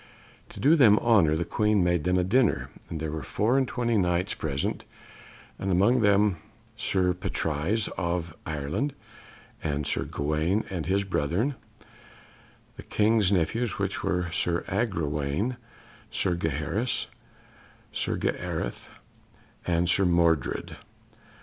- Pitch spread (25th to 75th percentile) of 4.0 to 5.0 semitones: Yes, average, 4.6 semitones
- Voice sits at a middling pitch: No, very low, 90 Hz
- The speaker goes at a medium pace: No, slow, 125 wpm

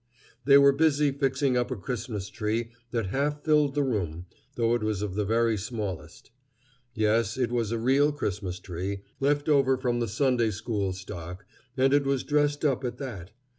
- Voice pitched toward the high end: No, low, 120 Hz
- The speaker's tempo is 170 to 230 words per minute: Yes, average, 180 wpm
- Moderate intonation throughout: Yes, average, 4.9 semitones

